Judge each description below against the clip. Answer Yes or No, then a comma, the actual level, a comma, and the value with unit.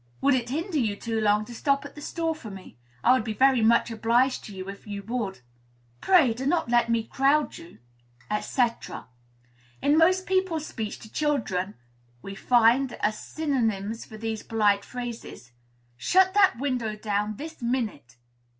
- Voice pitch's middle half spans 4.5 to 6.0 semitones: Yes, average, 4.8 semitones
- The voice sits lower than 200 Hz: No, high, 235 Hz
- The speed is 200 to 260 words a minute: No, average, 170 wpm